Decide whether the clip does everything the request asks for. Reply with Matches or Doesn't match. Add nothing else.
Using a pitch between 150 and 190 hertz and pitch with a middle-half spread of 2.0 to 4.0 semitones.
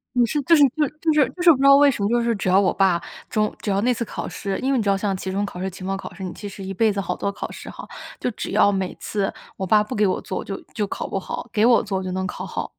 Doesn't match